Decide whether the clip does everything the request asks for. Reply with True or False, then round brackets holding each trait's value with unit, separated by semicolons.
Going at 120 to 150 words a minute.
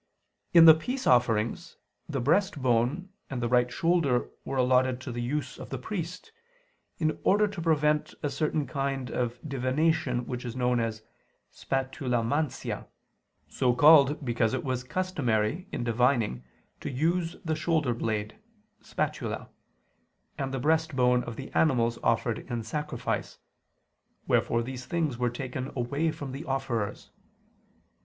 True (140 wpm)